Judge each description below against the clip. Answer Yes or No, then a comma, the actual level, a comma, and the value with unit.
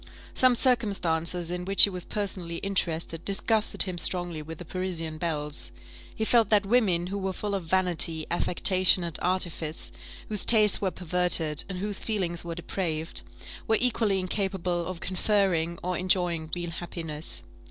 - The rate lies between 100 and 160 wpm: Yes, average, 150 wpm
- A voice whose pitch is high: No, medium, 180 Hz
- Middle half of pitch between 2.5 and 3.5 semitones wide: Yes, average, 2.8 semitones